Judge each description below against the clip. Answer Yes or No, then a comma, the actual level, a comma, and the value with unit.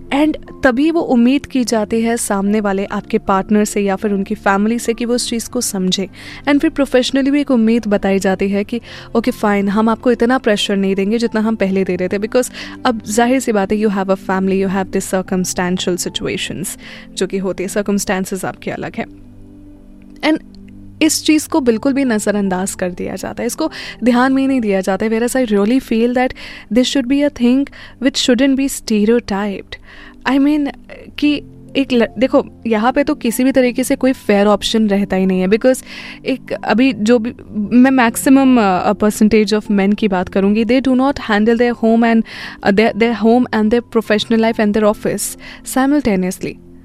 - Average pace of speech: No, fast, 195 wpm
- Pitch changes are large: No, average, 4.1 semitones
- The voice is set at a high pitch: Yes, high, 225 Hz